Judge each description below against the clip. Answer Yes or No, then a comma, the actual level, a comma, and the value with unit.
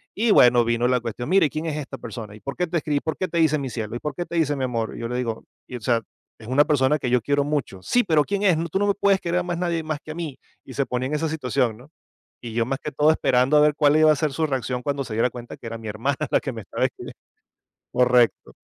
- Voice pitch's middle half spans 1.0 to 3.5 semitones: No, average, 4.3 semitones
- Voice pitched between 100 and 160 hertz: Yes, medium, 140 Hz